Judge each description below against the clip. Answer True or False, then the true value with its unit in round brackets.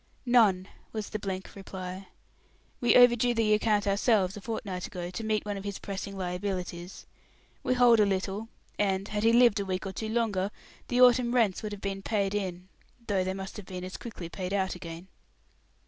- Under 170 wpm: False (195 wpm)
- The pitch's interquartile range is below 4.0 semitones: True (2.7 semitones)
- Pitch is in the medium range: False (200 Hz)